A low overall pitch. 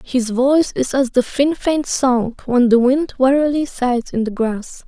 No: very high, 260 Hz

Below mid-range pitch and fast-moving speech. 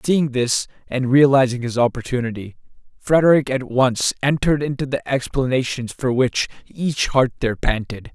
No: low, 130 Hz; average, 140 wpm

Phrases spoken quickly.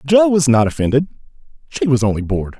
No: average, 185 wpm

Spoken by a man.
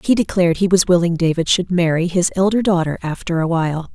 No: female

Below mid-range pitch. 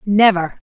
No: high, 195 Hz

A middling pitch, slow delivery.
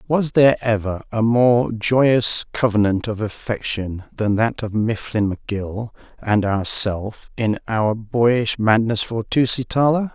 No: low, 110 Hz; slow, 130 wpm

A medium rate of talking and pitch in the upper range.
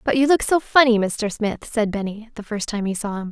No: fast, 270 wpm; high, 225 Hz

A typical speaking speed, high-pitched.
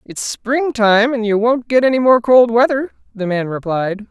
Yes: average, 190 wpm; high, 230 Hz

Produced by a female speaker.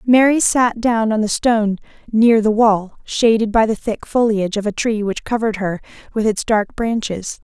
Yes: female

